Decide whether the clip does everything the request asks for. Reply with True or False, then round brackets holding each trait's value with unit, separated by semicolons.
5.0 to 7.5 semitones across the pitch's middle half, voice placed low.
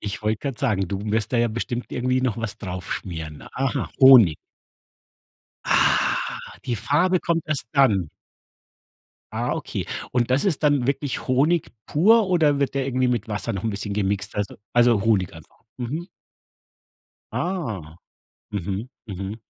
True (5.5 semitones; 120 Hz)